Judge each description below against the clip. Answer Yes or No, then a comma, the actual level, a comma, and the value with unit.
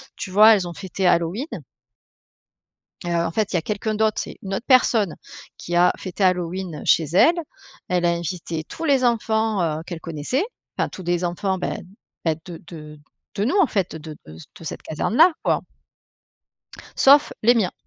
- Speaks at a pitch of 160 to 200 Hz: Yes, medium, 185 Hz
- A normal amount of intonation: Yes, average, 4.6 semitones